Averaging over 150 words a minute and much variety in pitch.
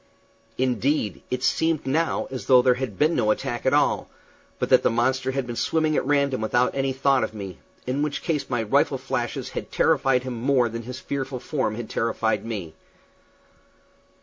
No: average, 185 wpm; average, 3.0 semitones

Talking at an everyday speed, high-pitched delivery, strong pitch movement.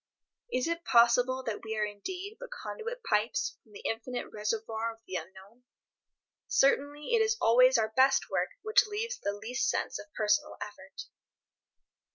Yes: average, 160 wpm; high, 245 Hz; wide, 7.6 semitones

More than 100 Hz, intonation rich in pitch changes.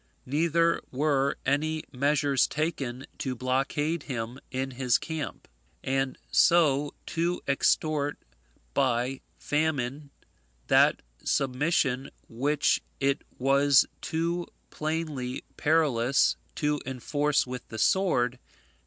No: medium, 140 Hz; average, 3.1 semitones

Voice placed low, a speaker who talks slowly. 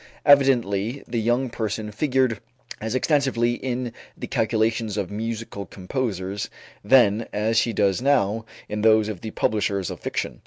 No: low, 110 Hz; average, 145 wpm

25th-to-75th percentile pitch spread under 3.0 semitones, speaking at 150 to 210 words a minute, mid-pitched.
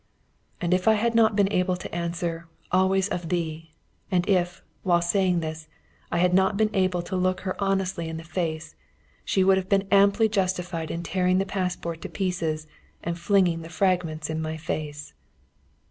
Yes: narrow, 2.5 semitones; average, 180 wpm; medium, 180 Hz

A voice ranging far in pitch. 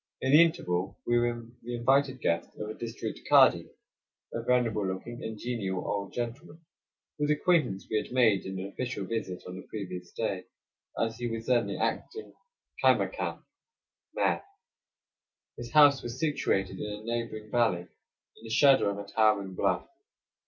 No: average, 3.7 semitones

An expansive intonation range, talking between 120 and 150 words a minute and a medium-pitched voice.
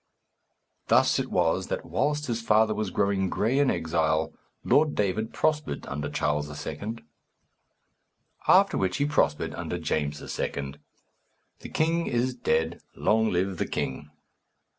No: wide, 7.3 semitones; slow, 135 wpm; low, 100 Hz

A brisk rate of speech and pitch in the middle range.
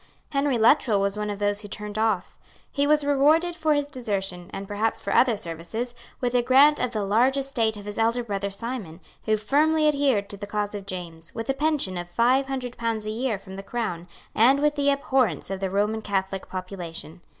No: fast, 210 wpm; high, 220 Hz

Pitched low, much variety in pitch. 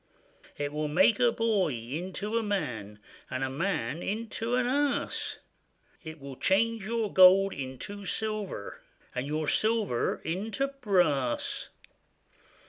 No: high, 190 Hz; wide, 7.4 semitones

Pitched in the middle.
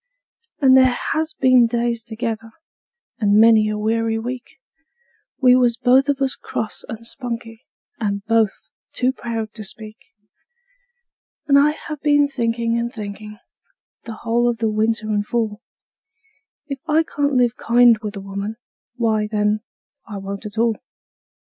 No: high, 230 Hz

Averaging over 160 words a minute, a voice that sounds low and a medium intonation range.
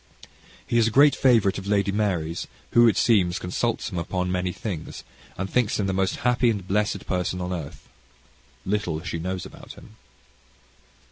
Yes: average, 175 wpm; very low, 95 Hz; average, 3.2 semitones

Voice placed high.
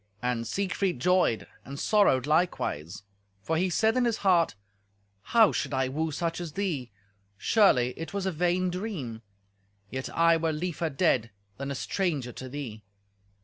No: medium, 165 Hz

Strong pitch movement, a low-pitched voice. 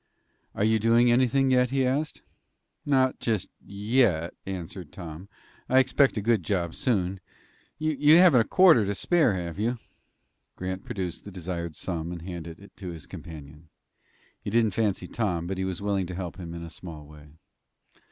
Yes: wide, 5.8 semitones; very low, 95 Hz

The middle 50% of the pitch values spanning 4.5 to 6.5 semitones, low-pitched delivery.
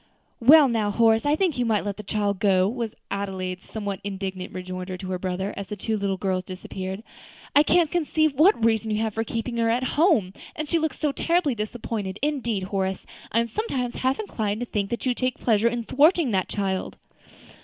No: average, 4.9 semitones; high, 220 Hz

